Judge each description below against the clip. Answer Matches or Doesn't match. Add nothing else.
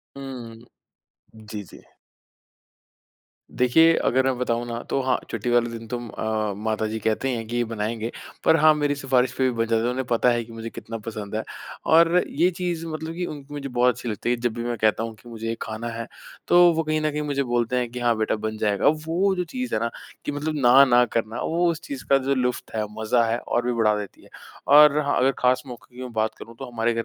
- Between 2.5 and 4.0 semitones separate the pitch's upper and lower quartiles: Matches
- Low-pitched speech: Matches